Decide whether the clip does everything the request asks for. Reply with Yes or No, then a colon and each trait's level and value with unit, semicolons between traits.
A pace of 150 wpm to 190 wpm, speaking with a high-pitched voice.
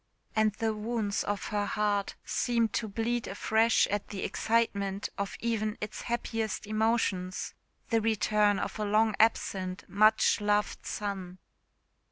No: slow, 135 wpm; high, 210 Hz